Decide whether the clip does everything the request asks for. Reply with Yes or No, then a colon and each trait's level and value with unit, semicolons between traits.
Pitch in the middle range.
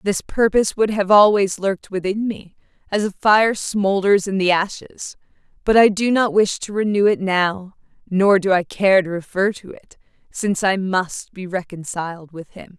No: high, 195 Hz